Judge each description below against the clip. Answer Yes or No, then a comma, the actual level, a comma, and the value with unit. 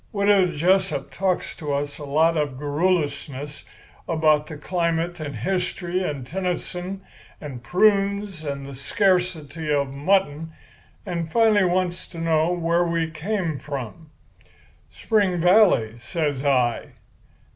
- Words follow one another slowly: Yes, slow, 125 wpm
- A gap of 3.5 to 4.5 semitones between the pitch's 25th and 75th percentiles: Yes, average, 4.0 semitones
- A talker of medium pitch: Yes, medium, 165 Hz